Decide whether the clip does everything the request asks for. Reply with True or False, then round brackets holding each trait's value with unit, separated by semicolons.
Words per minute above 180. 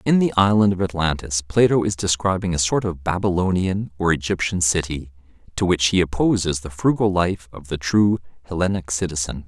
False (170 wpm)